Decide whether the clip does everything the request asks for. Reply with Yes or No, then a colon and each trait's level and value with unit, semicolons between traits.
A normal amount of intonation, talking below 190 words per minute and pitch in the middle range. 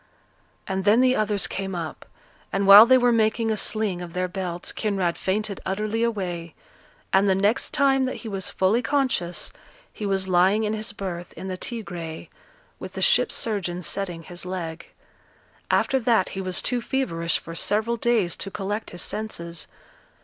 No: average, 3.7 semitones; average, 170 wpm; high, 195 Hz